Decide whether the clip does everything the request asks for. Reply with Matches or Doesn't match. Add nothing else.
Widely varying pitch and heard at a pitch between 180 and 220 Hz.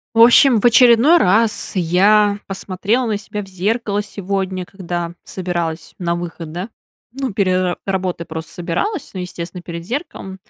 Doesn't match